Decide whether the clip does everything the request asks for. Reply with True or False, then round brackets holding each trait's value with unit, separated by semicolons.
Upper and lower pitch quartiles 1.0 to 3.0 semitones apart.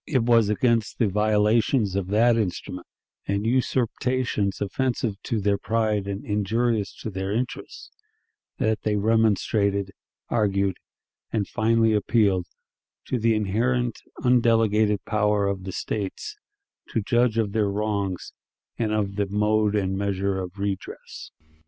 True (2.4 semitones)